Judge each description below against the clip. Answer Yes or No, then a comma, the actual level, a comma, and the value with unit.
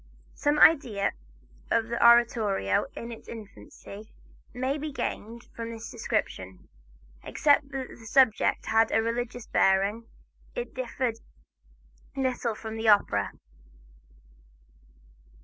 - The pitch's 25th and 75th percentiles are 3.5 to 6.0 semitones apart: No, average, 2.8 semitones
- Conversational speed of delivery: No, slow, 110 wpm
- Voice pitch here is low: No, high, 230 Hz